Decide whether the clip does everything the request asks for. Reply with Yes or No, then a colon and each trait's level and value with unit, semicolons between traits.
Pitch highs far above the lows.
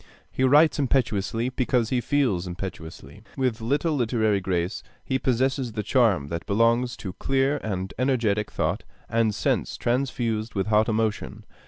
No: average, 4.3 semitones